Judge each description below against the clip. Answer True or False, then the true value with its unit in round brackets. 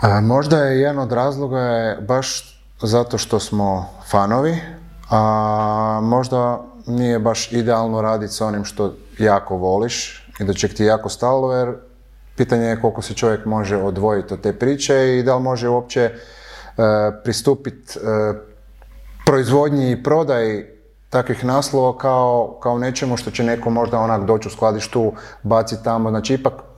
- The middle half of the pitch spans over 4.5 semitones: False (2.9 semitones)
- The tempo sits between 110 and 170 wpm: True (150 wpm)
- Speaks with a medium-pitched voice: False (115 Hz)